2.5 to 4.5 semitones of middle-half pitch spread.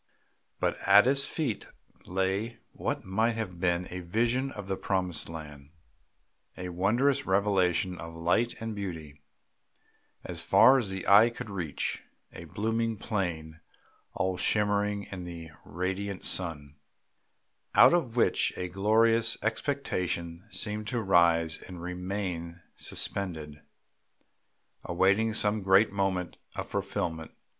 Yes: average, 4.1 semitones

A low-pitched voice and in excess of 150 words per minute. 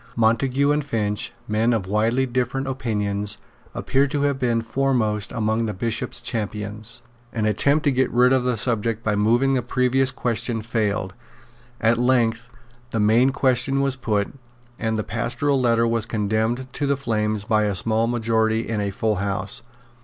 Yes: low, 115 Hz; average, 165 wpm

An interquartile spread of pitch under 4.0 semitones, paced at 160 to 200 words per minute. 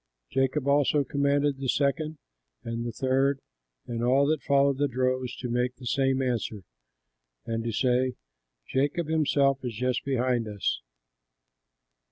No: narrow, 2.4 semitones; average, 145 wpm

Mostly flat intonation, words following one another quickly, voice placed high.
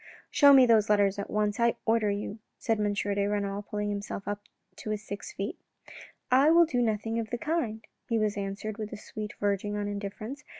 Yes: narrow, 2.1 semitones; fast, 215 wpm; high, 210 Hz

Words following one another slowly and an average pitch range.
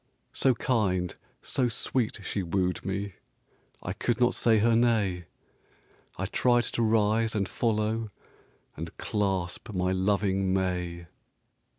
Yes: slow, 120 wpm; average, 3.5 semitones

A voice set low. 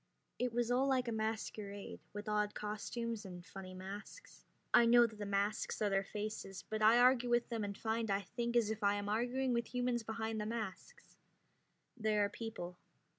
No: high, 220 Hz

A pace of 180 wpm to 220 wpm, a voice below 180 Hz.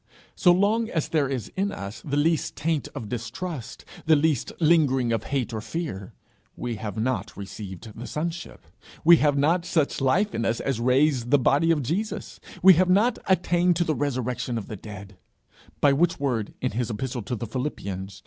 Yes: average, 190 wpm; medium, 140 Hz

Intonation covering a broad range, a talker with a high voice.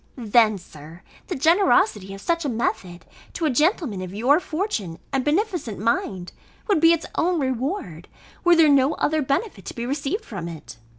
Yes: wide, 8.8 semitones; very high, 265 Hz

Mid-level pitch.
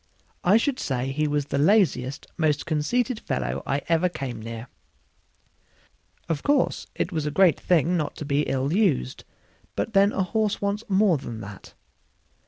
Yes: medium, 155 Hz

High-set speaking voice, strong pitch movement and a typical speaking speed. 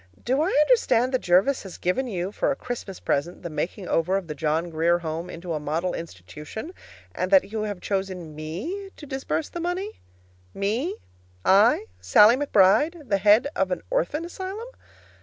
Yes: high, 195 Hz; wide, 8.5 semitones; average, 175 wpm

